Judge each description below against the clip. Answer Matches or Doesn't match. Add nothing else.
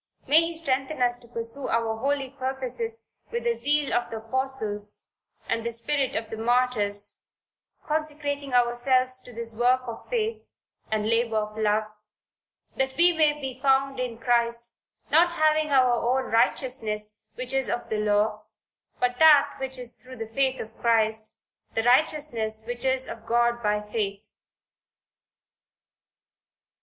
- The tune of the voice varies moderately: Matches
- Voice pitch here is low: Doesn't match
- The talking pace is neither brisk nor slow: Matches